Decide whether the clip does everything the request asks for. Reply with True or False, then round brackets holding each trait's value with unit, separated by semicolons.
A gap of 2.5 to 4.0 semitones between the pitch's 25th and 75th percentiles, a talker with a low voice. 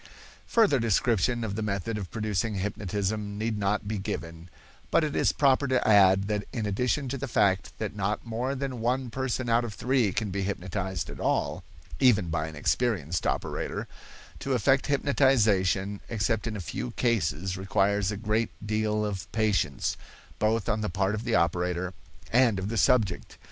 True (3.6 semitones; 105 Hz)